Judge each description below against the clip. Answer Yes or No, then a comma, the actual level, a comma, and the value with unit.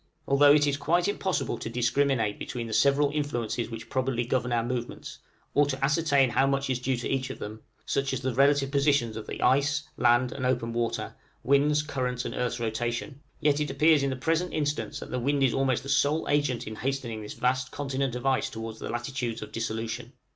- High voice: No, low, 130 Hz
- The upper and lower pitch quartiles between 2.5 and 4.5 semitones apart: Yes, average, 3.1 semitones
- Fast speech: Yes, fast, 210 wpm